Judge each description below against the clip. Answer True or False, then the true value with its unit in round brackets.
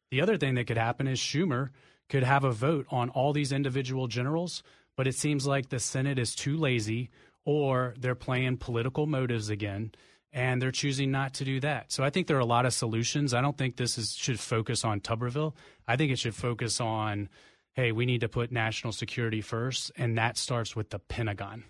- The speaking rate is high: True (215 wpm)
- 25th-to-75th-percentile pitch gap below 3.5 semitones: True (3.0 semitones)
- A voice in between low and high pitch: False (125 Hz)